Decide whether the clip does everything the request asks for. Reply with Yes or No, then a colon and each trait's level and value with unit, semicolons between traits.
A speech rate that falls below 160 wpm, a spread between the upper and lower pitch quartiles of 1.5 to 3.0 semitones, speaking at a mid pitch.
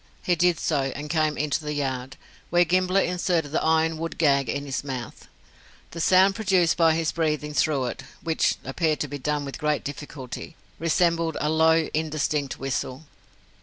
No: average, 170 wpm; narrow, 2.6 semitones; medium, 155 Hz